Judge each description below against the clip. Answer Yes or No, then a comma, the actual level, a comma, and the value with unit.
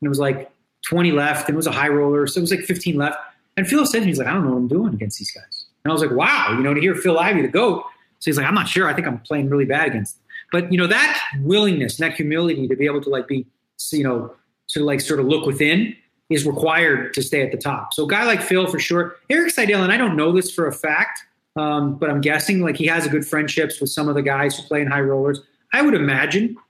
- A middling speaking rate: No, fast, 290 wpm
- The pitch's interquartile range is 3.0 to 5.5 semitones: Yes, average, 4.3 semitones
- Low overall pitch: No, medium, 155 Hz